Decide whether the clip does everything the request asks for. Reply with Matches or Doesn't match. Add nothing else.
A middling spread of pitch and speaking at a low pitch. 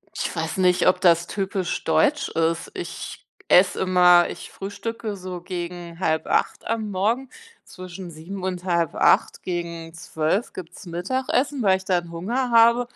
Doesn't match